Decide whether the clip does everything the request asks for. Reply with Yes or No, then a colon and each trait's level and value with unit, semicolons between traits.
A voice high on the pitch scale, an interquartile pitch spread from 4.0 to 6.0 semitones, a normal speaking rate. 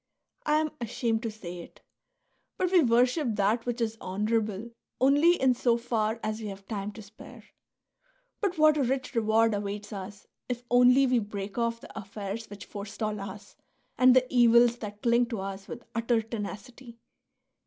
No: high, 230 Hz; average, 3.0 semitones; average, 170 wpm